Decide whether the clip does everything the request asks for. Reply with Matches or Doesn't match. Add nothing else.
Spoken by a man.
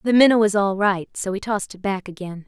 Doesn't match